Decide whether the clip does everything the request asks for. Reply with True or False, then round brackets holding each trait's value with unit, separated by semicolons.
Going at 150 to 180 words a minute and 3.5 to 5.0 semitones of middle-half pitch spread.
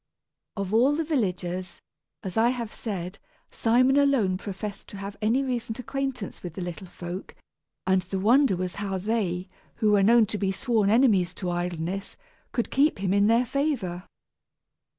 True (165 wpm; 4.4 semitones)